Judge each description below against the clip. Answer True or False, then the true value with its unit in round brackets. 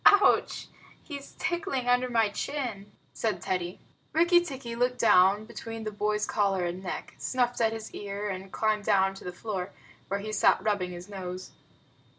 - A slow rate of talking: False (165 wpm)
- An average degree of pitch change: True (4.0 semitones)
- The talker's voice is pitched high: True (210 Hz)